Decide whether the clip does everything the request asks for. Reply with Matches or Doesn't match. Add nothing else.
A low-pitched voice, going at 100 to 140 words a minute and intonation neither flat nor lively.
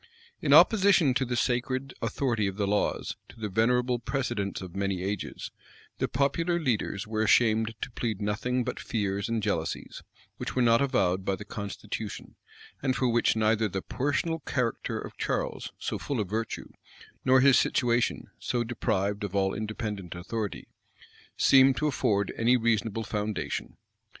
Doesn't match